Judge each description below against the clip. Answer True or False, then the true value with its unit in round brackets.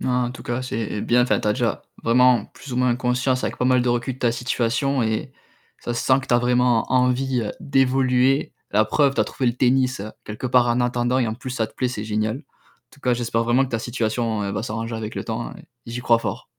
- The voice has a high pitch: False (125 Hz)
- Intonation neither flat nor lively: False (1.8 semitones)